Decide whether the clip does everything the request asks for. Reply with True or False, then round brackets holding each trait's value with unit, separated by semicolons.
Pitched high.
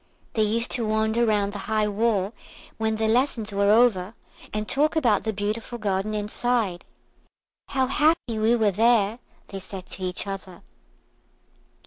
True (215 Hz)